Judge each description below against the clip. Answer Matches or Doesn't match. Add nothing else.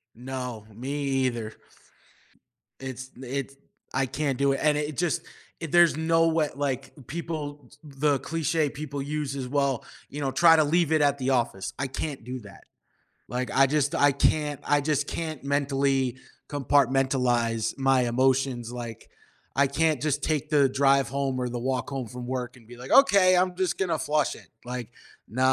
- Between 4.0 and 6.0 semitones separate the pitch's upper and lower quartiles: Doesn't match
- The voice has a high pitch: Doesn't match